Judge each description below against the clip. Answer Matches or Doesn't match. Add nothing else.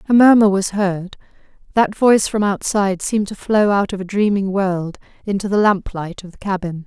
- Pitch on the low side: Doesn't match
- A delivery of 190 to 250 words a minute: Matches